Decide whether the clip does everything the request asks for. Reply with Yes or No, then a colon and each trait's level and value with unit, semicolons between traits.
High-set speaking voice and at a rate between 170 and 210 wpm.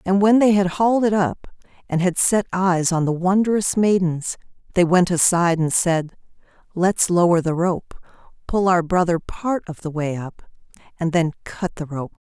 No: medium, 180 Hz; average, 180 wpm